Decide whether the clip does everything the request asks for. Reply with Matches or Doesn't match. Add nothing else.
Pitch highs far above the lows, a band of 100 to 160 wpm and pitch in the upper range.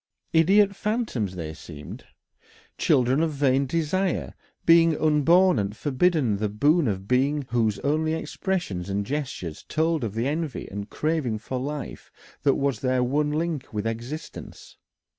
Doesn't match